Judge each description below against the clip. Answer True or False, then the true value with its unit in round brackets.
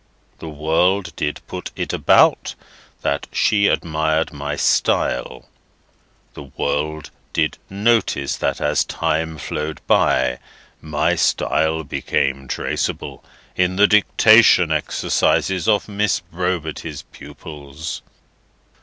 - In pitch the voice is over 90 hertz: False (80 Hz)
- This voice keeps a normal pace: False (100 wpm)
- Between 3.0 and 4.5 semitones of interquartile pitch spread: True (3.8 semitones)